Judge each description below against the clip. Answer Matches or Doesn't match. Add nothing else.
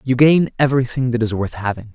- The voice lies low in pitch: Matches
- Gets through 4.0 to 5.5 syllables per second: Doesn't match